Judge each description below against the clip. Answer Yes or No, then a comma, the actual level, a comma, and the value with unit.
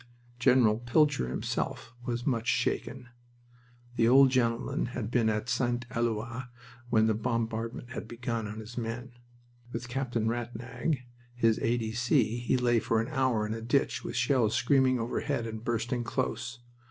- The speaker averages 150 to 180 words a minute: Yes, average, 155 wpm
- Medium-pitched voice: No, low, 120 Hz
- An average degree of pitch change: No, narrow, 1.5 semitones